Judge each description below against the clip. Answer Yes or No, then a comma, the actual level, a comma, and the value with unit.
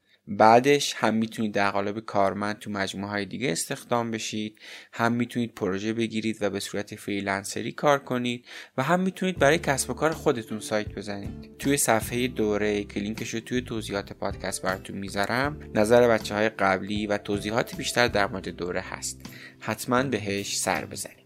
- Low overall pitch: Yes, low, 110 Hz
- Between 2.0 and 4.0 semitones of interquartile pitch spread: Yes, average, 3.2 semitones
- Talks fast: Yes, fast, 165 wpm